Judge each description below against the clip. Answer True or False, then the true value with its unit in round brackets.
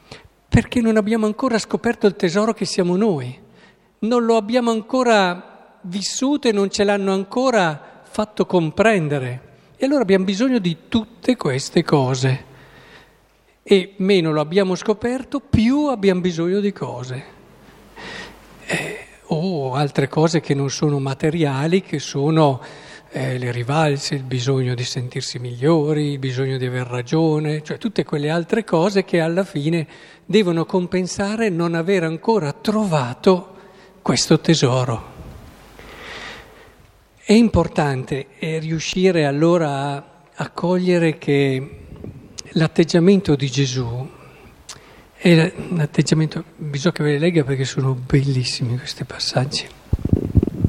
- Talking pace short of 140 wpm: True (120 wpm)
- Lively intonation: True (5.9 semitones)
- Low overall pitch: False (165 Hz)